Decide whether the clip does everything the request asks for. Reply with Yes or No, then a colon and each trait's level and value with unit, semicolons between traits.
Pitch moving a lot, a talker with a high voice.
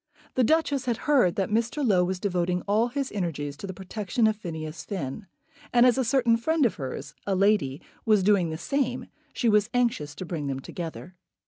Yes: wide, 5.7 semitones; high, 205 Hz